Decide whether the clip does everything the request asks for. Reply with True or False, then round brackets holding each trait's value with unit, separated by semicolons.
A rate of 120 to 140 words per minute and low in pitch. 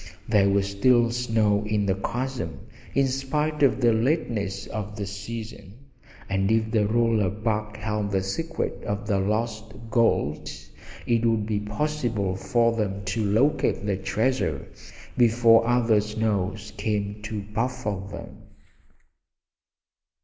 True (135 wpm; 110 Hz)